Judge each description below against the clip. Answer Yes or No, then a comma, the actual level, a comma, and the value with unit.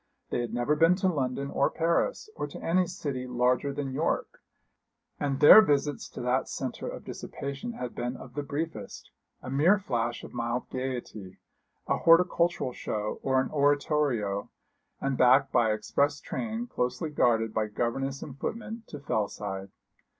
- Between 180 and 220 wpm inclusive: No, average, 155 wpm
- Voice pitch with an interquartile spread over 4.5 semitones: No, average, 4.0 semitones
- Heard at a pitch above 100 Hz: Yes, low, 135 Hz